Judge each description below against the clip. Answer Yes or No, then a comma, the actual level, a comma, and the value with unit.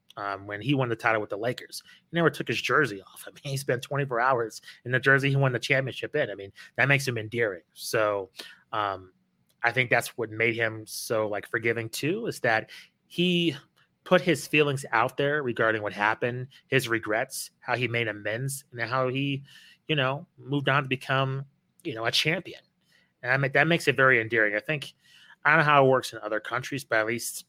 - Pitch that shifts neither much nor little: Yes, average, 3.9 semitones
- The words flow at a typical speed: No, fast, 210 wpm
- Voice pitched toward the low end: Yes, low, 130 Hz